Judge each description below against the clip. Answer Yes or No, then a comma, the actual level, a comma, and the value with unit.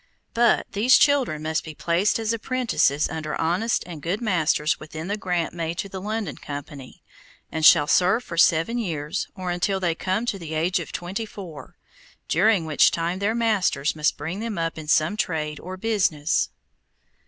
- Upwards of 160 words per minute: Yes, average, 175 wpm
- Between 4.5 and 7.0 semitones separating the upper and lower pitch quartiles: Yes, average, 5.0 semitones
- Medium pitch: Yes, medium, 175 Hz